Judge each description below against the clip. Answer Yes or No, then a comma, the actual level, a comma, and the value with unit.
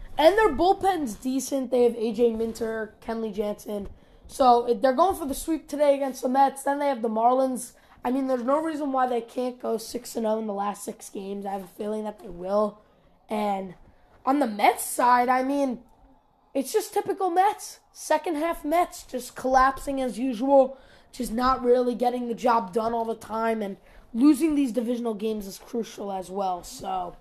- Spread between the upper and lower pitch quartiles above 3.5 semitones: Yes, average, 4.1 semitones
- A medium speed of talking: Yes, average, 190 wpm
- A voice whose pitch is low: No, high, 245 Hz